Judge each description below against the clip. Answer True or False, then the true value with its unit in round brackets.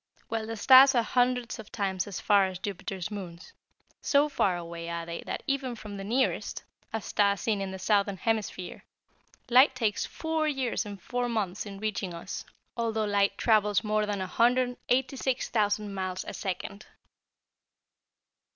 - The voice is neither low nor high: False (210 Hz)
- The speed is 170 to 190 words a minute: False (160 wpm)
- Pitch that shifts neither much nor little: True (4.0 semitones)